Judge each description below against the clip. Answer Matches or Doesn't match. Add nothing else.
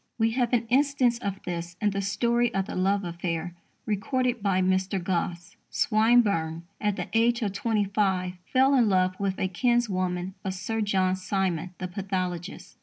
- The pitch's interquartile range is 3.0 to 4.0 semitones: Matches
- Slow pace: Doesn't match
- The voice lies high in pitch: Matches